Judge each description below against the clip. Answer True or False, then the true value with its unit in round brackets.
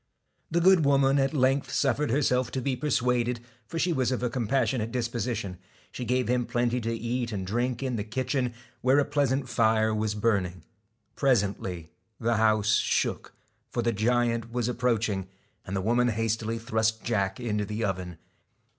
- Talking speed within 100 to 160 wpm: False (170 wpm)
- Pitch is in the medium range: False (120 Hz)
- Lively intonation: False (2.8 semitones)